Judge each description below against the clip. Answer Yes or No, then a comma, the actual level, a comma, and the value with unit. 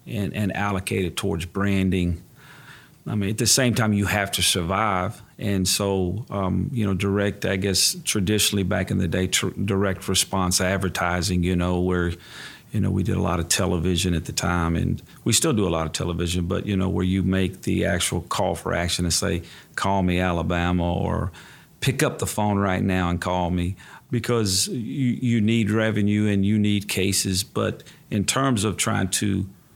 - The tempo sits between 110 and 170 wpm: No, average, 195 wpm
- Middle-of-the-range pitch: No, very low, 95 Hz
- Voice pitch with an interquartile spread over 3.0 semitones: No, narrow, 2.6 semitones